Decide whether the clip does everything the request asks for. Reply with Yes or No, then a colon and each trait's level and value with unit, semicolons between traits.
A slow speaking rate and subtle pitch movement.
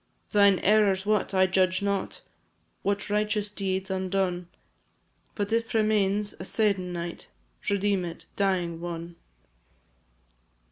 Yes: slow, 105 wpm; narrow, 1.9 semitones